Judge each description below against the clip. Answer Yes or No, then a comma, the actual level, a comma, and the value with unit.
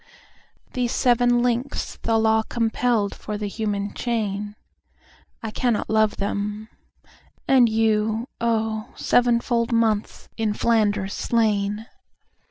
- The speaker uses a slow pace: Yes, slow, 95 wpm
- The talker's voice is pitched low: No, high, 220 Hz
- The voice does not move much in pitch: Yes, narrow, 1.9 semitones